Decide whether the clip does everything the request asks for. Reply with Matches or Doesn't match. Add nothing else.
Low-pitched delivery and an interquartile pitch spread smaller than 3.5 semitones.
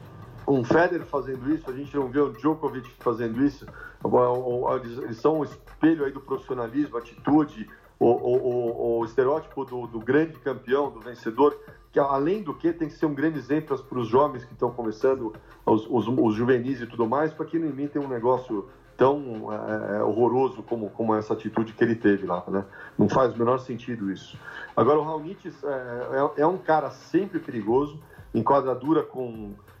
Doesn't match